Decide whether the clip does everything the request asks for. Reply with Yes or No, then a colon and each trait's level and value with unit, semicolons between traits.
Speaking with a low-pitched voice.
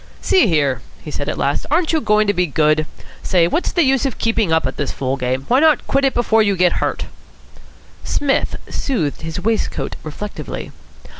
No: high, 190 Hz